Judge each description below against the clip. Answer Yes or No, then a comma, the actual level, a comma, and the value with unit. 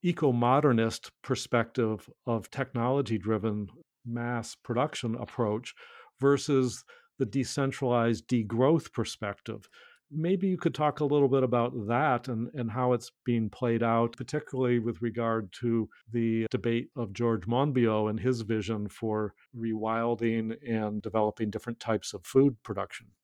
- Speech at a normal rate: No, slow, 130 wpm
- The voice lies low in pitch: Yes, low, 120 Hz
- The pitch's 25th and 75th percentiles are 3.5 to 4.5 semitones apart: No, narrow, 2.5 semitones